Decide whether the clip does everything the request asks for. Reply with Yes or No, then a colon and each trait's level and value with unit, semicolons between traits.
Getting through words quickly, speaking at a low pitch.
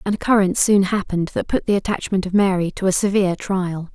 No: fast, 215 wpm; high, 190 Hz